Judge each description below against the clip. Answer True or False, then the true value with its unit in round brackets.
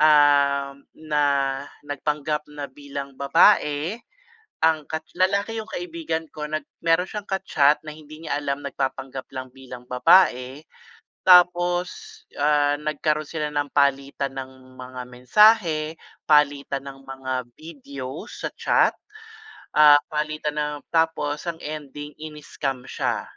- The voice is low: False (150 Hz)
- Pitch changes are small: True (2.2 semitones)